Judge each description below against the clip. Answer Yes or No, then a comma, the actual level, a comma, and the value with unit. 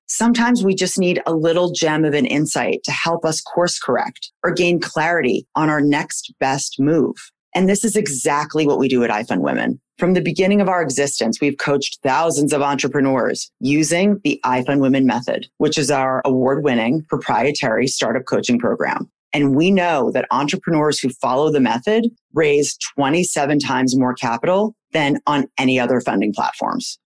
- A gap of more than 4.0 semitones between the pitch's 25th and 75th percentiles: Yes, average, 4.5 semitones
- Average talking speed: Yes, average, 170 wpm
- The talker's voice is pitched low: No, medium, 150 Hz